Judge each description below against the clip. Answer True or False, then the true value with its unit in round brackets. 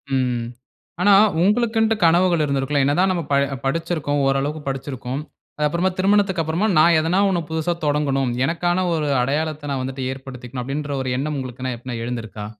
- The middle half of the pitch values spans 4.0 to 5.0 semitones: True (4.4 semitones)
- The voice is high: False (150 Hz)